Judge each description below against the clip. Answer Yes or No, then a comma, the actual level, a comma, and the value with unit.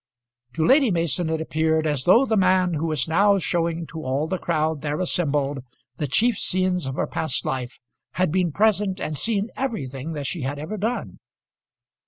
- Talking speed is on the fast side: No, average, 185 wpm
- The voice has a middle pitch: Yes, medium, 165 Hz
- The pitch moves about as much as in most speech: Yes, average, 4.0 semitones